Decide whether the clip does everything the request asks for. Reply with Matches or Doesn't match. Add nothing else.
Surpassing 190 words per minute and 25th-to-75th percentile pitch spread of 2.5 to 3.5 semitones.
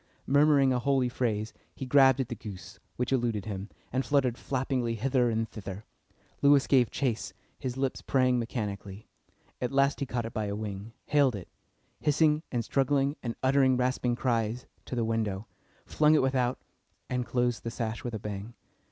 Doesn't match